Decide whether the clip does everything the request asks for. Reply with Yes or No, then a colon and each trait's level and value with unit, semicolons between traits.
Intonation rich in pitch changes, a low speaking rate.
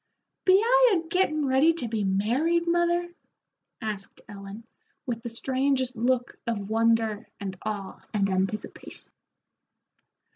Yes: wide, 7.7 semitones; slow, 120 wpm